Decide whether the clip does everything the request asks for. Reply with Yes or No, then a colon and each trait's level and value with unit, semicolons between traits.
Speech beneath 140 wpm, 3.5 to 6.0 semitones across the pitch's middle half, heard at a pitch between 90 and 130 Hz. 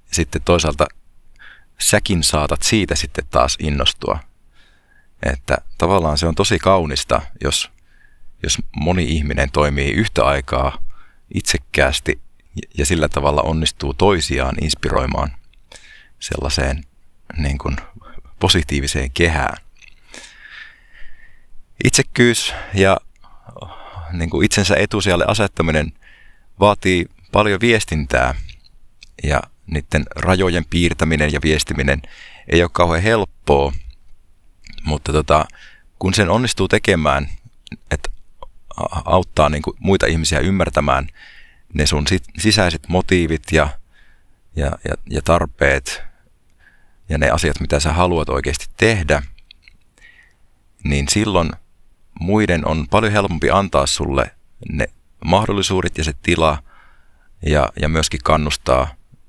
No: average, 100 wpm; average, 4.1 semitones; very low, 80 Hz